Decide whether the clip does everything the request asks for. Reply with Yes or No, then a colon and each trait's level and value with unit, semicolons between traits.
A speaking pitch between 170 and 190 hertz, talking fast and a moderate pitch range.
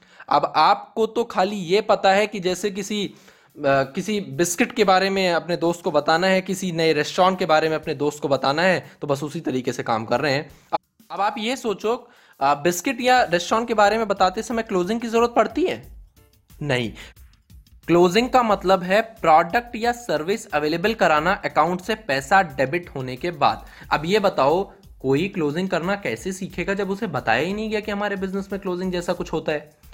Yes: medium, 185 Hz; fast, 200 wpm; average, 5.0 semitones